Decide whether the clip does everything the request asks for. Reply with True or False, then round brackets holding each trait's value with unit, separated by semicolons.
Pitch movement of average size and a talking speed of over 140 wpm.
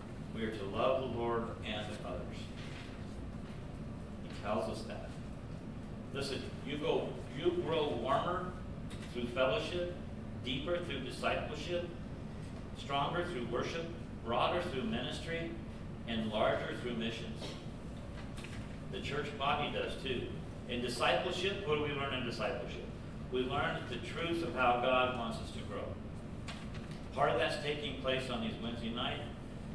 False (3.4 semitones; 135 wpm)